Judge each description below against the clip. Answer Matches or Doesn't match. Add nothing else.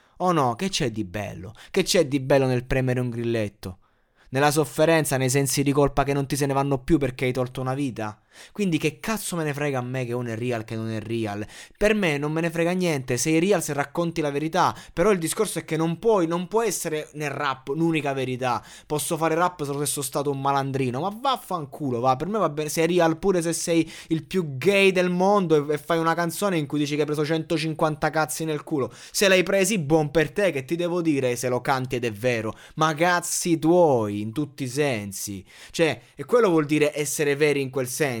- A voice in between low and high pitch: Matches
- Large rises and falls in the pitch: Doesn't match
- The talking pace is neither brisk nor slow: Doesn't match